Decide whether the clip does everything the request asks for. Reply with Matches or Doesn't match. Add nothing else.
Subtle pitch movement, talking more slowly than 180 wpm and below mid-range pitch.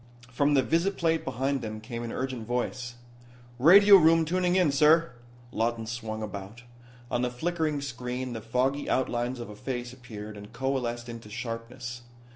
Doesn't match